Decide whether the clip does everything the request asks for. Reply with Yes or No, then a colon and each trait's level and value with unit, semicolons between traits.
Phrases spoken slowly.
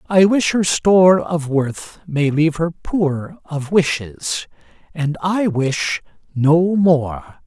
Yes: slow, 130 wpm